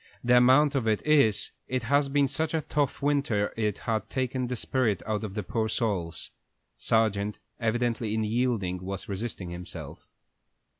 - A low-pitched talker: Yes, low, 115 Hz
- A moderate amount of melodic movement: Yes, average, 3.9 semitones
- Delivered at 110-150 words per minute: No, average, 160 wpm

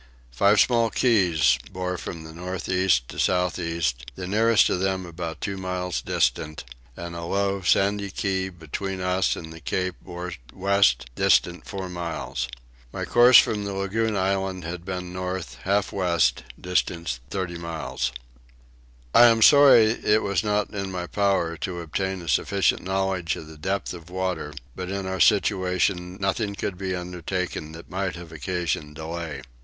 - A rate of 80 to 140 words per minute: No, average, 160 wpm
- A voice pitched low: Yes, very low, 90 Hz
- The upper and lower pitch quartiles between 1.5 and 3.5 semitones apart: Yes, narrow, 2.6 semitones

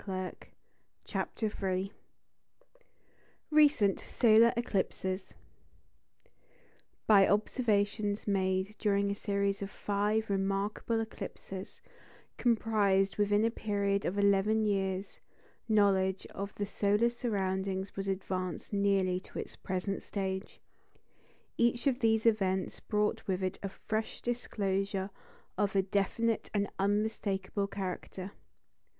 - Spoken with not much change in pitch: Yes, narrow, 1.9 semitones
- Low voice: No, high, 200 Hz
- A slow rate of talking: Yes, slow, 105 wpm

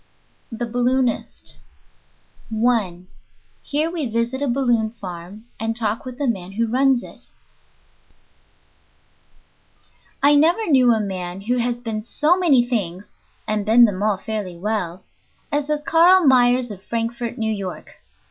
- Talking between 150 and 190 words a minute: No, average, 140 wpm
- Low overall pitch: No, high, 235 Hz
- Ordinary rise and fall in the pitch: Yes, average, 3.8 semitones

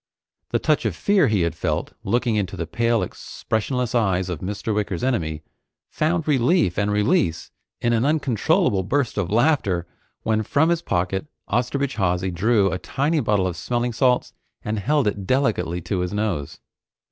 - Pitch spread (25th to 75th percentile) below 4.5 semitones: No, wide, 5.5 semitones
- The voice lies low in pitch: Yes, low, 110 Hz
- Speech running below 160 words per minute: No, average, 165 wpm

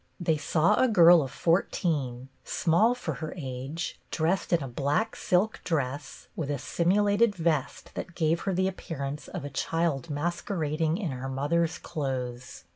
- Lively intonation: No, average, 3.9 semitones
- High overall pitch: No, medium, 160 Hz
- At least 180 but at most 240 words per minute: No, average, 155 wpm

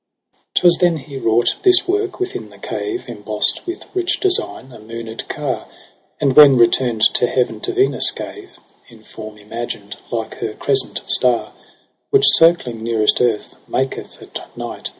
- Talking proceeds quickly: No, average, 155 wpm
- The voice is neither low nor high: No, low, 130 Hz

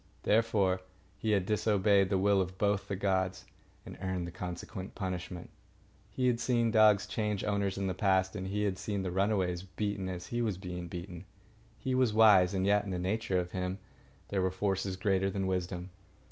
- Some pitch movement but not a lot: No, narrow, 2.0 semitones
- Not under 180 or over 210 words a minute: Yes, average, 190 wpm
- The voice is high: No, very low, 95 Hz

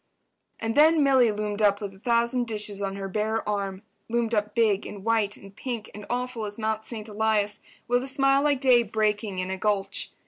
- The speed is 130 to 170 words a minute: No, average, 195 wpm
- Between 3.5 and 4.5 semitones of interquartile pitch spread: No, narrow, 2.5 semitones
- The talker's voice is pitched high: Yes, high, 215 Hz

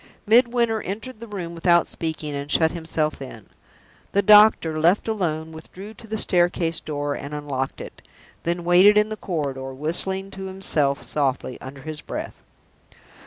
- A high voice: No, medium, 170 Hz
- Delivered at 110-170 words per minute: Yes, average, 155 wpm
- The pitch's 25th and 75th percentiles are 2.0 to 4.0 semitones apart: No, average, 5.2 semitones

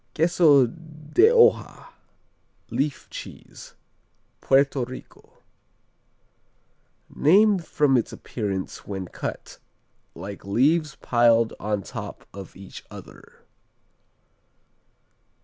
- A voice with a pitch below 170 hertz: Yes, low, 135 Hz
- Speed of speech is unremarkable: No, slow, 80 wpm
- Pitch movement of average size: No, wide, 6.9 semitones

